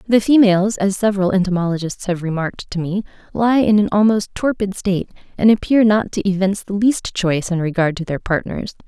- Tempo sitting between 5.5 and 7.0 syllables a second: Yes, 5.9 syllables/s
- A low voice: No, high, 195 Hz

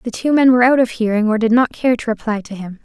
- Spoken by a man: No, female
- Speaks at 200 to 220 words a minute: No, fast, 315 wpm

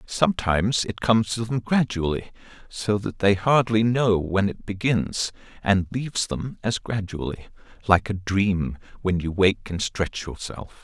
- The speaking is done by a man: Yes, male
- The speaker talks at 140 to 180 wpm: Yes, average, 155 wpm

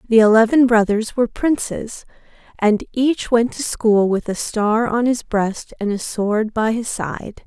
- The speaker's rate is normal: Yes, average, 175 wpm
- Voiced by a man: No, female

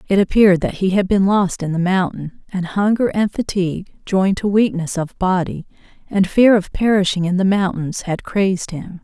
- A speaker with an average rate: Yes, average, 195 wpm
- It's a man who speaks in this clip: No, female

